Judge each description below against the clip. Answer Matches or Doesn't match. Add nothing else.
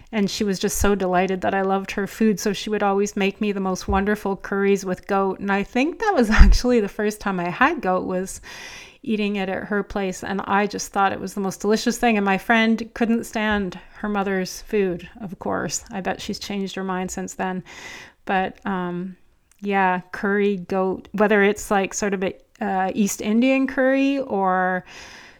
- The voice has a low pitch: Doesn't match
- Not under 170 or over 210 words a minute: Matches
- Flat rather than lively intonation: Matches